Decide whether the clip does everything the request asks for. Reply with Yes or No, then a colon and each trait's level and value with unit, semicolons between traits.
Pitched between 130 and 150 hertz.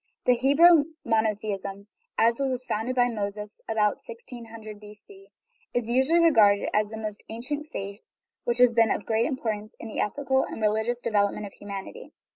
No: high, 225 Hz